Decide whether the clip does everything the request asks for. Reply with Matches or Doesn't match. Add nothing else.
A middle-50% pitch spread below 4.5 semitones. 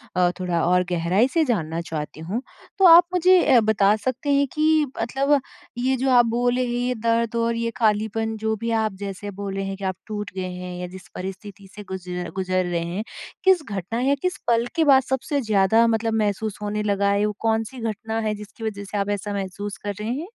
Matches